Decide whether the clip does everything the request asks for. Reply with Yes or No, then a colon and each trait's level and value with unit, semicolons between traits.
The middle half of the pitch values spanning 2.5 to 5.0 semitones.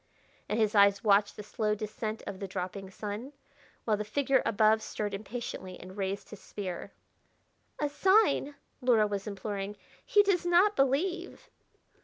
No: wide, 5.4 semitones